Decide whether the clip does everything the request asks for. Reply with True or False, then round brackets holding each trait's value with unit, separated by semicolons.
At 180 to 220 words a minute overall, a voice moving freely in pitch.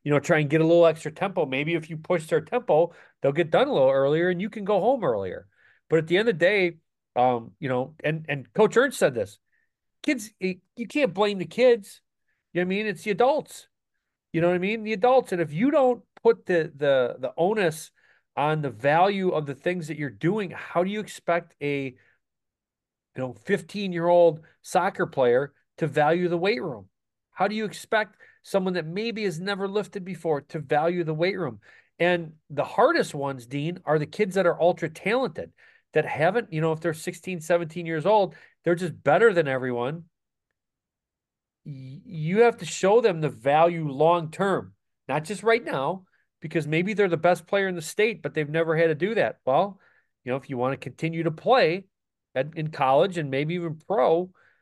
False (205 wpm; 4.6 semitones)